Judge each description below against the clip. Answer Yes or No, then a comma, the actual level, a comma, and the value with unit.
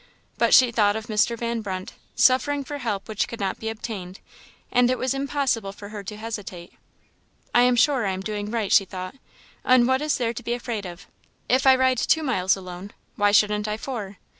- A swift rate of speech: Yes, fast, 210 wpm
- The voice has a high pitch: Yes, high, 220 Hz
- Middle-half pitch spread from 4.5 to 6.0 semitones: No, average, 3.8 semitones